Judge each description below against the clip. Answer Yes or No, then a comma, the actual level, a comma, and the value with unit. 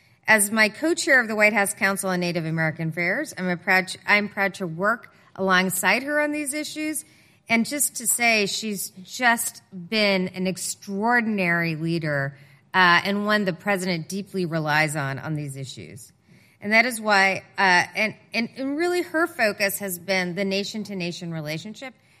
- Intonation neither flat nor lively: Yes, average, 3.8 semitones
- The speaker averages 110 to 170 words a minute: Yes, average, 165 wpm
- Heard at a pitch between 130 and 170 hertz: No, high, 195 Hz